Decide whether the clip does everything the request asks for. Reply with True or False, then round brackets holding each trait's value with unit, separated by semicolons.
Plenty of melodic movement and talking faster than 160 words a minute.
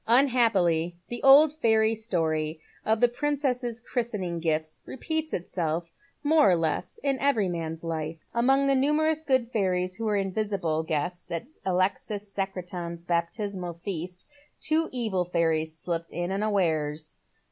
False (6.1 semitones; 135 wpm)